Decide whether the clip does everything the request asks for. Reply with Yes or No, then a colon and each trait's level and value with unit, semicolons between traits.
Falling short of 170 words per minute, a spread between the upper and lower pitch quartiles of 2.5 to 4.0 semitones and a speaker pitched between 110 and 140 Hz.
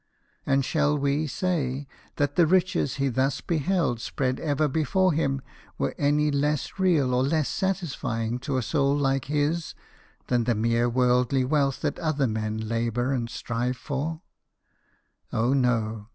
Yes: average, 150 wpm; average, 3.5 semitones; low, 135 Hz